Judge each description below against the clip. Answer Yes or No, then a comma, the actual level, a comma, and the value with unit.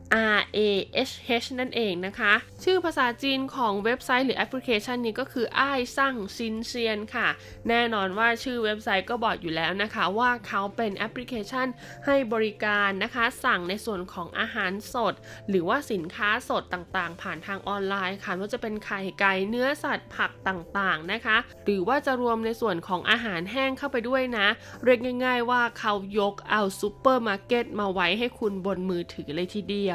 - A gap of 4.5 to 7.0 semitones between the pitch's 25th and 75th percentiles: No, average, 3.8 semitones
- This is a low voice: No, high, 220 Hz